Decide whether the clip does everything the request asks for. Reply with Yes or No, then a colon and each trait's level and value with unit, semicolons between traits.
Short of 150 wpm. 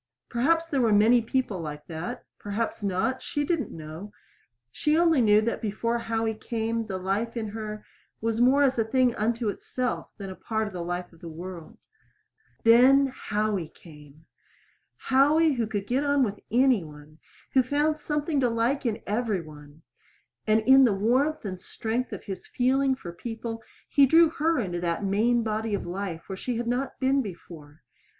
No: average, 180 wpm